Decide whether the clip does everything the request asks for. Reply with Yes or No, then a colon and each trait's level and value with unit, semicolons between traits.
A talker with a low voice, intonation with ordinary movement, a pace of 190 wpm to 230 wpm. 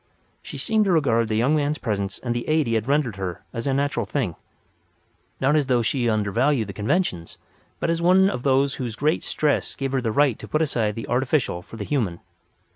Yes: low, 130 Hz; average, 4.9 semitones; average, 200 wpm